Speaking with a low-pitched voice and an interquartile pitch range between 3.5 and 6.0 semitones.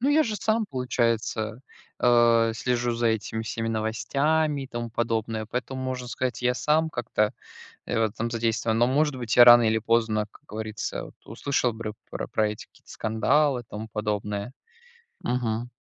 No: low, 120 Hz; narrow, 2.5 semitones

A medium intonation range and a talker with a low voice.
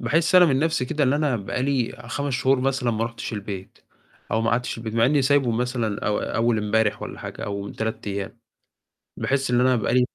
Yes: average, 3.3 semitones; low, 120 Hz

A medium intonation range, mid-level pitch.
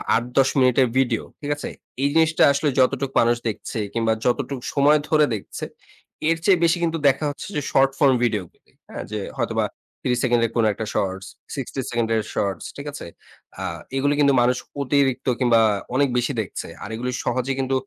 No: average, 3.4 semitones; low, 130 Hz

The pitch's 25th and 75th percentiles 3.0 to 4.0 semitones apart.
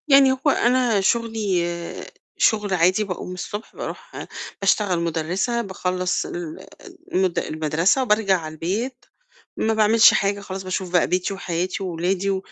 Yes: average, 3.5 semitones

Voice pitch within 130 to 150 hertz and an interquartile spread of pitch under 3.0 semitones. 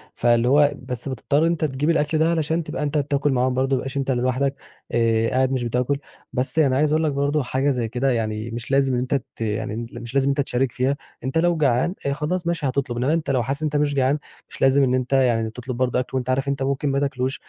Yes: low, 135 Hz; narrow, 2.4 semitones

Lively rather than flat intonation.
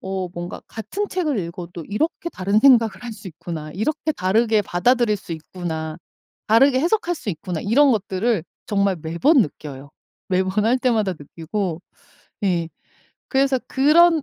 Yes: wide, 6.7 semitones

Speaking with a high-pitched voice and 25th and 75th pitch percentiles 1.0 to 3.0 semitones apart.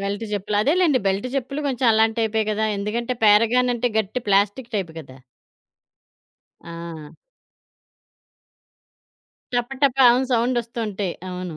No: high, 220 Hz; average, 3.7 semitones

